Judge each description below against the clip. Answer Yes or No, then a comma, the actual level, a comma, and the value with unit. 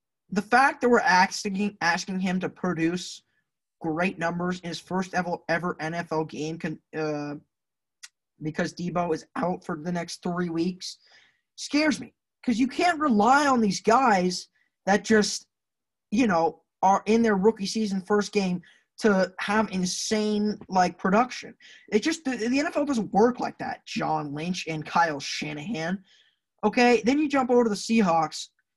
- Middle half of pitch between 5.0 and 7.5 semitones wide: No, average, 4.6 semitones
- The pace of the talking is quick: No, average, 155 wpm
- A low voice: No, high, 190 Hz